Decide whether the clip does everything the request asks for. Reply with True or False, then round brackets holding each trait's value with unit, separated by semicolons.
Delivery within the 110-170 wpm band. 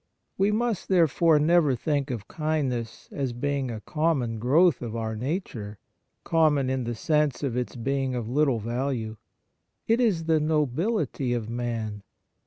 True (150 wpm)